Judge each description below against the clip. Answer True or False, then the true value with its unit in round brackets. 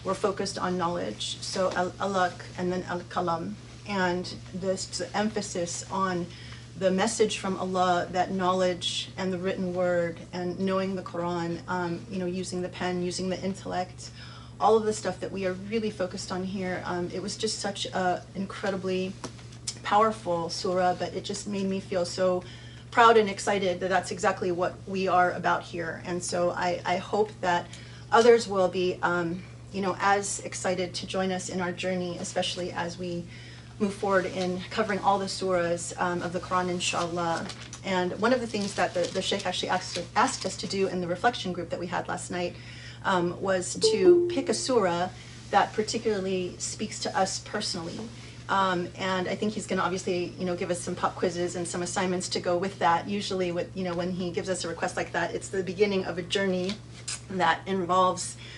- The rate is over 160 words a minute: True (190 wpm)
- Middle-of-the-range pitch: True (180 Hz)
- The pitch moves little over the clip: True (1.5 semitones)